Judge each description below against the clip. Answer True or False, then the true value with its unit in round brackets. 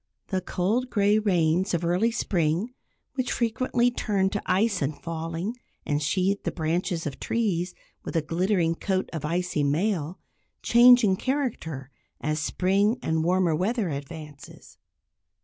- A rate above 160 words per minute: False (145 wpm)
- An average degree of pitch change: True (4.7 semitones)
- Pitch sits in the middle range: True (180 Hz)